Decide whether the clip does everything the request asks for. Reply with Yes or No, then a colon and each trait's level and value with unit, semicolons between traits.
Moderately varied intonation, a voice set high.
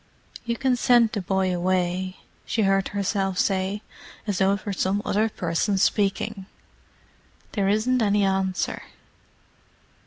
No: narrow, 2.1 semitones; high, 195 Hz